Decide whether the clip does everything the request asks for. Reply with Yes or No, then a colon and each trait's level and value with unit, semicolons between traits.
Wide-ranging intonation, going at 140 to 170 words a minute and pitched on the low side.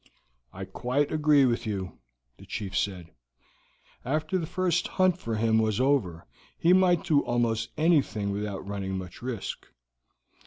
Yes: wide, 7.3 semitones; average, 145 wpm; low, 120 Hz